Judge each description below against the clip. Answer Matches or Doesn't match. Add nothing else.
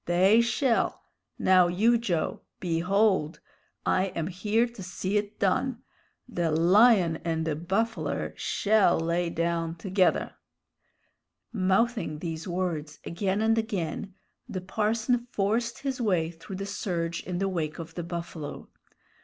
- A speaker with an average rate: Doesn't match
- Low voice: Doesn't match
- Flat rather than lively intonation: Doesn't match